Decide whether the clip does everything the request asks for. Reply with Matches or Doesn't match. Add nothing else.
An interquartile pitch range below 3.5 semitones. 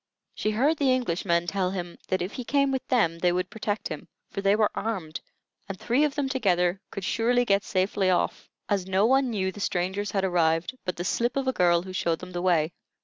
Doesn't match